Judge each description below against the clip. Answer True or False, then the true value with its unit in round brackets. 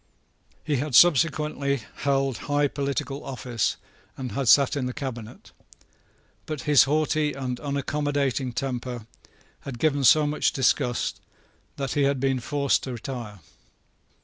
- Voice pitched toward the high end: False (140 Hz)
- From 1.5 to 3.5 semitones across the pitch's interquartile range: True (2.4 semitones)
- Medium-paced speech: False (130 wpm)